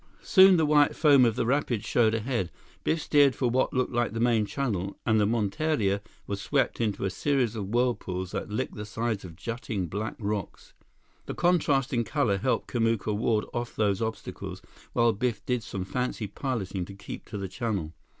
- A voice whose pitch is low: Yes, low, 115 Hz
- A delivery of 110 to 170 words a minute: No, average, 190 wpm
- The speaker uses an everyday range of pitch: Yes, average, 3.9 semitones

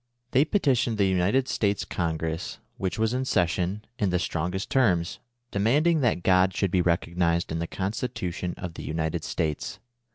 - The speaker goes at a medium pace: Yes, average, 160 wpm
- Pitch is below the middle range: Yes, very low, 95 Hz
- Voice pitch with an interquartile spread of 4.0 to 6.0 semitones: Yes, average, 4.6 semitones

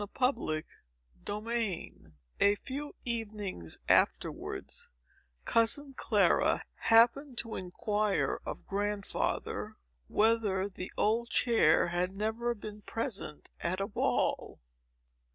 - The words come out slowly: Yes, slow, 95 wpm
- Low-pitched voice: No, high, 215 Hz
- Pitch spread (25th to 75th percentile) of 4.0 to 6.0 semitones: No, average, 3.1 semitones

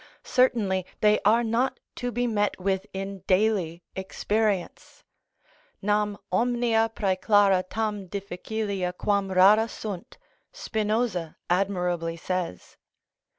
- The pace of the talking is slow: Yes, slow, 100 wpm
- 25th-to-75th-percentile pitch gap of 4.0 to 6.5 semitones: No, average, 2.9 semitones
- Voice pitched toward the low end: No, high, 200 Hz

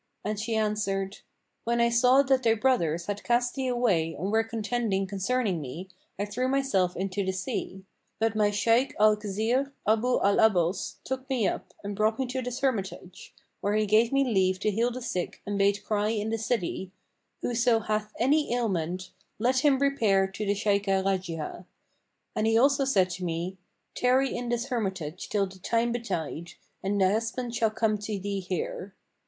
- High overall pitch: Yes, high, 215 Hz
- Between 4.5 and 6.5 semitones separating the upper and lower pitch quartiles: No, average, 3.9 semitones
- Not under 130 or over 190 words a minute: Yes, average, 180 wpm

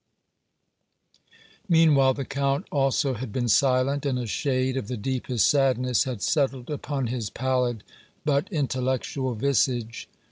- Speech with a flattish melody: Yes, narrow, 1.9 semitones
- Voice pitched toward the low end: Yes, low, 130 Hz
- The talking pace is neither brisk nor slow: No, slow, 130 wpm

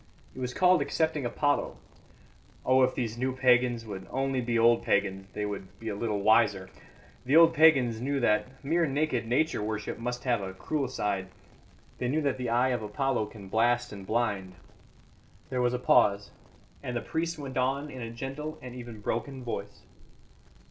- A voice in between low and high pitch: No, low, 120 Hz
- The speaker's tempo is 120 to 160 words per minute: No, average, 180 wpm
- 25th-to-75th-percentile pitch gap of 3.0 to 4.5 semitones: Yes, average, 3.7 semitones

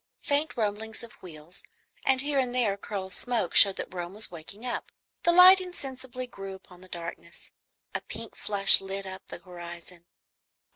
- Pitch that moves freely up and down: Yes, wide, 5.7 semitones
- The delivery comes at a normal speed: Yes, average, 180 wpm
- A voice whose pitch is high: Yes, high, 200 Hz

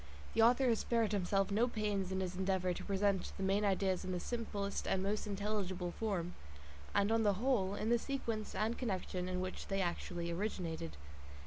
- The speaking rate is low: No, average, 190 wpm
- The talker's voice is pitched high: Yes, high, 200 Hz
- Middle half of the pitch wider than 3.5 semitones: No, narrow, 2.6 semitones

